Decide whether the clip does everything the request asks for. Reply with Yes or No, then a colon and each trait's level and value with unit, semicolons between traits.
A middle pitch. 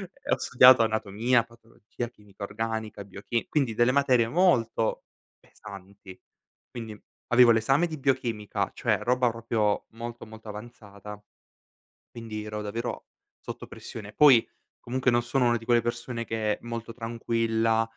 No: low, 115 Hz